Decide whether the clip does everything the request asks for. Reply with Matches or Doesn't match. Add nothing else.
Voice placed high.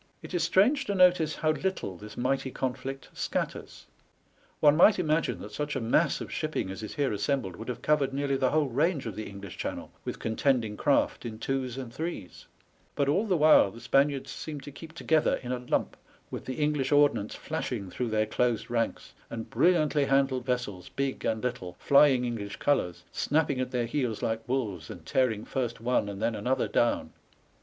Doesn't match